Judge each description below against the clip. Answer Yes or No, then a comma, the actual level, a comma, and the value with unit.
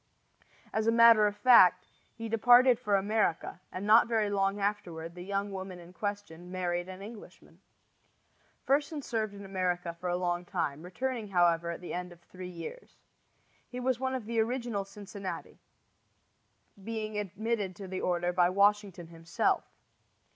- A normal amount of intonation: Yes, average, 3.7 semitones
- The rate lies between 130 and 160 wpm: Yes, average, 155 wpm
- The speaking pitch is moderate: No, high, 200 Hz